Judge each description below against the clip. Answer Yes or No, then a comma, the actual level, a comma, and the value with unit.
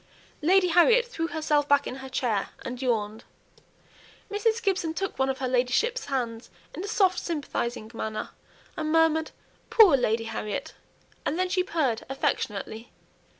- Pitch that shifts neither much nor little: No, wide, 7.0 semitones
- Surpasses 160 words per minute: No, average, 150 wpm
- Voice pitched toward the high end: Yes, very high, 290 Hz